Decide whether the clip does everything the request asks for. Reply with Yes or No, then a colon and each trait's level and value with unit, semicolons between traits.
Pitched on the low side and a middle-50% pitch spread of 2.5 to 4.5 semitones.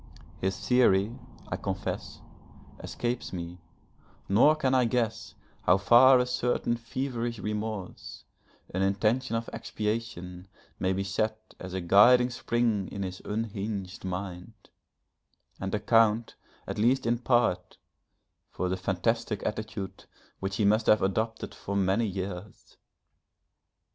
Yes: low, 105 Hz; average, 3.5 semitones